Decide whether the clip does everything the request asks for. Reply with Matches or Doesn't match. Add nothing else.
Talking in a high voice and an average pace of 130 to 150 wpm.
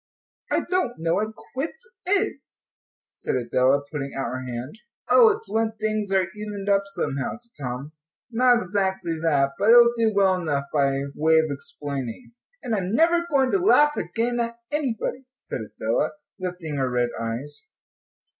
Doesn't match